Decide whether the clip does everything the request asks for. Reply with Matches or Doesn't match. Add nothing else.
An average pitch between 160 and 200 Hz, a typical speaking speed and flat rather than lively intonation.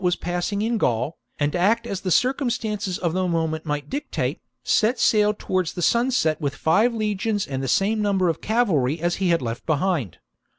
Doesn't match